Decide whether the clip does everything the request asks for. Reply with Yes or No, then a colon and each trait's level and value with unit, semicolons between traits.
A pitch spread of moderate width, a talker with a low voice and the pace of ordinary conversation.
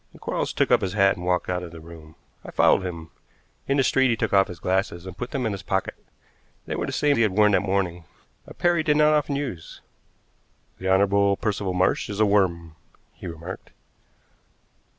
No: average, 3.7 semitones; very low, 95 Hz; fast, 215 wpm